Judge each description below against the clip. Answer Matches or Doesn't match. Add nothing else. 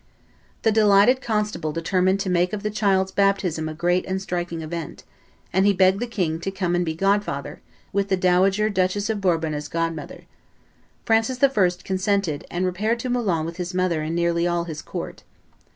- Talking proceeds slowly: Doesn't match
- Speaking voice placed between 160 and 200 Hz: Matches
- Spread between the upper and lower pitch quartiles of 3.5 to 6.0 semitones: Doesn't match